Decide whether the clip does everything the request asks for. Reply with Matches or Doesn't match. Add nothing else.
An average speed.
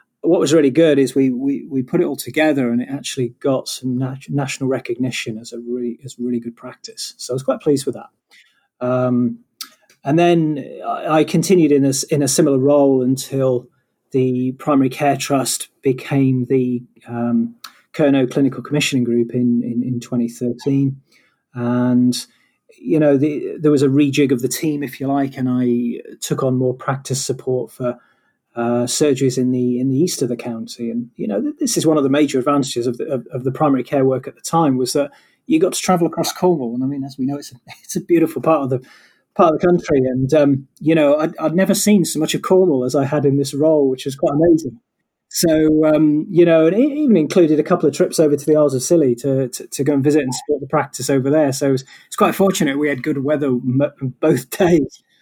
Doesn't match